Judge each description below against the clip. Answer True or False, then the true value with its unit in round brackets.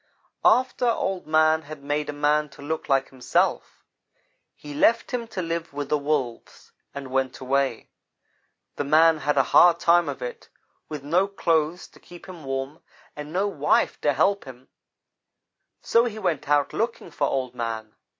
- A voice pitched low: False (150 Hz)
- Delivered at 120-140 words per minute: False (170 wpm)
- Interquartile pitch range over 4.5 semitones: False (3.8 semitones)